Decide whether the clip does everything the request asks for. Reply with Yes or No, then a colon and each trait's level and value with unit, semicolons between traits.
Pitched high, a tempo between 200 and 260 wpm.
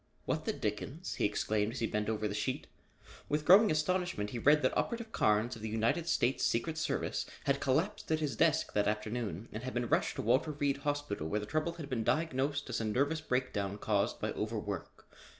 No: low, 130 Hz; fast, 205 wpm